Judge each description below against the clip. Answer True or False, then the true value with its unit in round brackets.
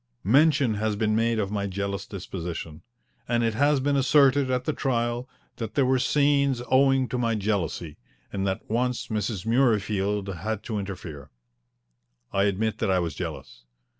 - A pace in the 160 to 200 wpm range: True (165 wpm)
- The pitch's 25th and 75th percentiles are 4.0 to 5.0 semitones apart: True (4.6 semitones)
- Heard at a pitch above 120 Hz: False (110 Hz)